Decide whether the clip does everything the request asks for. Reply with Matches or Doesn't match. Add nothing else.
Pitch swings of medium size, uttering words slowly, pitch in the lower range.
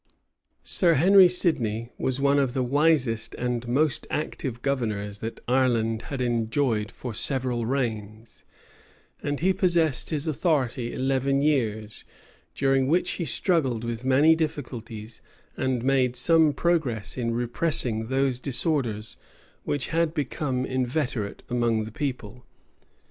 Matches